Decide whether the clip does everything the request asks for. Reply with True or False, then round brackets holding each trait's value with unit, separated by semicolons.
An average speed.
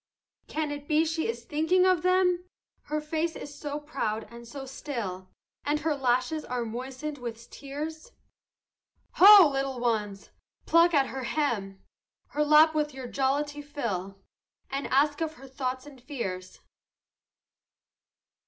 True (145 wpm)